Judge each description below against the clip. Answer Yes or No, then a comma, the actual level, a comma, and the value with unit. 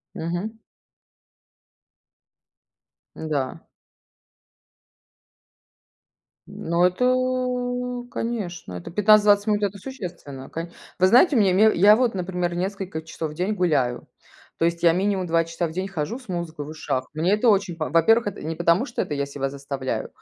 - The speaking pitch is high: No, medium, 180 Hz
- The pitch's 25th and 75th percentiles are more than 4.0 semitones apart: Yes, average, 4.8 semitones